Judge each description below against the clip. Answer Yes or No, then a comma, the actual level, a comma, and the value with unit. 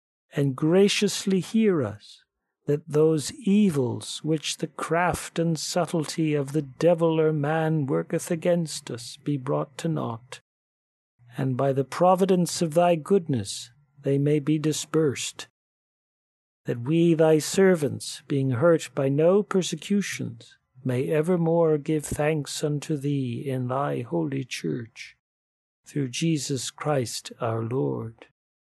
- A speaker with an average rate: No, slow, 125 wpm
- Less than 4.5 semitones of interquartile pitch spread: Yes, average, 3.8 semitones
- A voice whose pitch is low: No, medium, 150 Hz